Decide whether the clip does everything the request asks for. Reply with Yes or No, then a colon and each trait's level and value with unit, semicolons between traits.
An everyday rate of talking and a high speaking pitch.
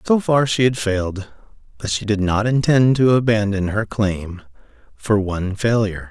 No: average, 165 wpm; low, 105 Hz